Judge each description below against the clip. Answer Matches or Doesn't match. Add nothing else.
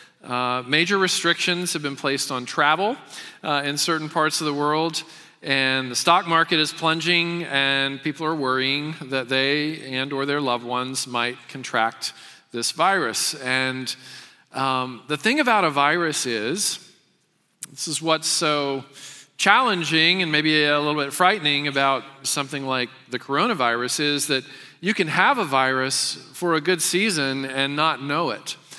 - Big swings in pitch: Doesn't match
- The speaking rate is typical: Matches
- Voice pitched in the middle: Matches